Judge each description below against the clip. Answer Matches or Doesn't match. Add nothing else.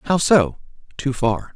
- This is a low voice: Matches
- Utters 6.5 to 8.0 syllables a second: Doesn't match